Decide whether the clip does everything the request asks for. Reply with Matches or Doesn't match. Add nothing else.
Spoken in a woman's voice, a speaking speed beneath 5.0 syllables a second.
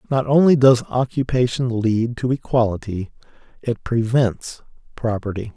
Doesn't match